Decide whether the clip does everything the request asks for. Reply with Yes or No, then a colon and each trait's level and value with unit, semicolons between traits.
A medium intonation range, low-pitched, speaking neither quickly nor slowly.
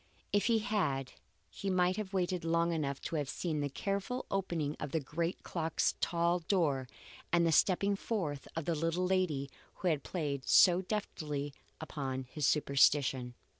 No: average, 4.4 semitones; medium, 165 Hz; average, 165 wpm